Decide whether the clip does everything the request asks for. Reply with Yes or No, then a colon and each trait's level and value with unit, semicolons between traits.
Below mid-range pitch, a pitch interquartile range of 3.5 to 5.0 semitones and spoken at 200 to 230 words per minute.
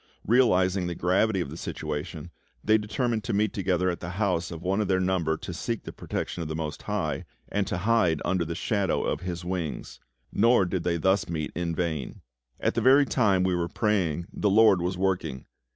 No: very low, 90 Hz; average, 3.1 semitones; fast, 205 wpm